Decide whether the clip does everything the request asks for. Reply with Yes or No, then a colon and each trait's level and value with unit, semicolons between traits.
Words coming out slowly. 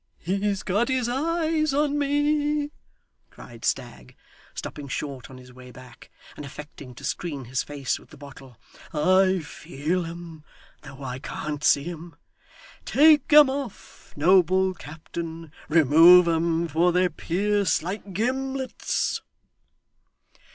Yes: slow, 125 wpm